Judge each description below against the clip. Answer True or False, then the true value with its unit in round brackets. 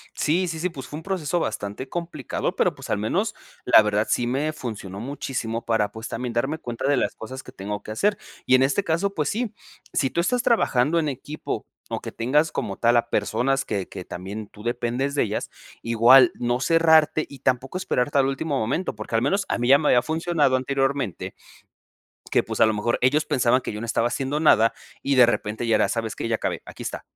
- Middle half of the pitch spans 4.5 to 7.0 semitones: True (5.0 semitones)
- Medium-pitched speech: False (130 Hz)